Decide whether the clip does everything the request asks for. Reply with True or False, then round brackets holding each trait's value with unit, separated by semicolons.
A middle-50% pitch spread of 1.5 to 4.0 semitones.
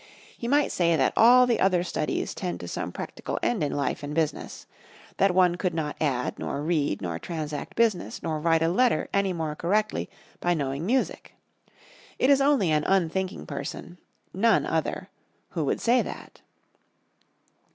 False (4.7 semitones)